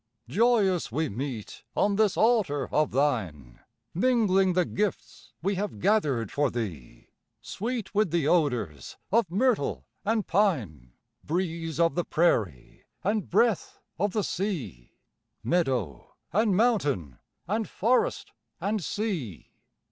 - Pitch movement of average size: No, wide, 8.8 semitones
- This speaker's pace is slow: Yes, slow, 120 wpm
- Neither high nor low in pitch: Yes, medium, 175 Hz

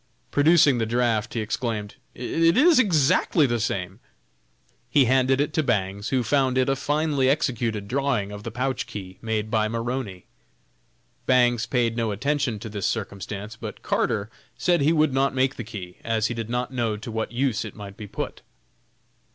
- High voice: No, low, 120 Hz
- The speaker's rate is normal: Yes, average, 175 wpm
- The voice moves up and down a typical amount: Yes, average, 4.0 semitones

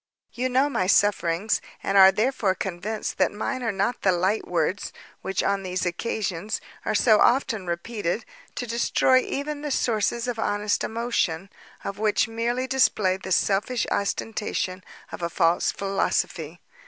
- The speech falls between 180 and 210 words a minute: No, average, 150 wpm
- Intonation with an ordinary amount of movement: Yes, average, 4.0 semitones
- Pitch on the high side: Yes, high, 205 Hz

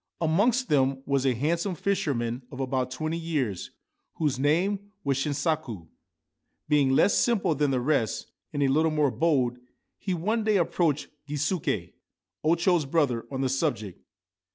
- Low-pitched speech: No, medium, 145 Hz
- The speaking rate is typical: Yes, average, 150 wpm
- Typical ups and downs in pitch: Yes, average, 4.2 semitones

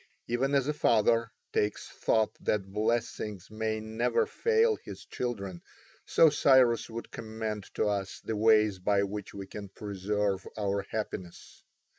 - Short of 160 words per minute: Yes, average, 140 wpm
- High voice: No, low, 110 Hz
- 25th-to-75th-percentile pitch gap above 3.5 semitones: No, narrow, 2.6 semitones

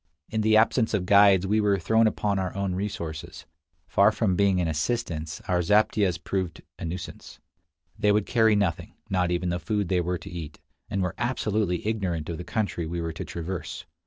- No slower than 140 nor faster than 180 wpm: No, average, 190 wpm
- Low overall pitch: Yes, very low, 95 Hz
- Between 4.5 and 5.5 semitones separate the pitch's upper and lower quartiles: No, average, 3.3 semitones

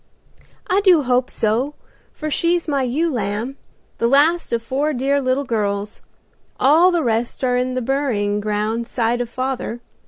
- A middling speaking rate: Yes, average, 160 wpm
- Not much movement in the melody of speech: No, average, 3.9 semitones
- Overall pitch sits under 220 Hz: No, very high, 255 Hz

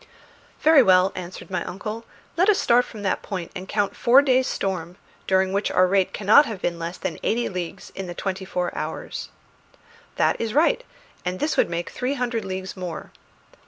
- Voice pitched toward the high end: Yes, high, 195 Hz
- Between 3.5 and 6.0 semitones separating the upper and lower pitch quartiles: Yes, average, 4.6 semitones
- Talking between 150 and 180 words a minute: No, average, 190 wpm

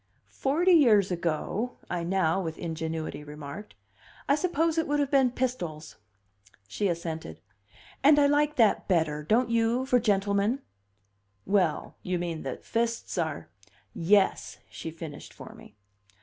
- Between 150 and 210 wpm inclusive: No, average, 140 wpm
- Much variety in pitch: Yes, wide, 7.6 semitones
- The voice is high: Yes, high, 195 Hz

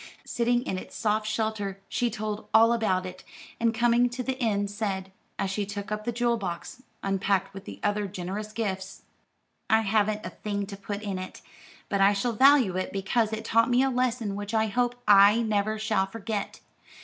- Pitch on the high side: Yes, high, 210 Hz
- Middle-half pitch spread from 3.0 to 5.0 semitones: No, narrow, 2.6 semitones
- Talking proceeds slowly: No, average, 195 wpm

